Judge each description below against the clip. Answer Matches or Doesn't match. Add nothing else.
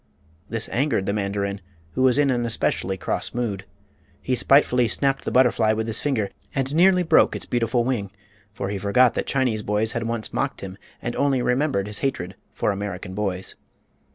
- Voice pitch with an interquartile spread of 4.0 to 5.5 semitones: Matches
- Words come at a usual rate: Matches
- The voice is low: Matches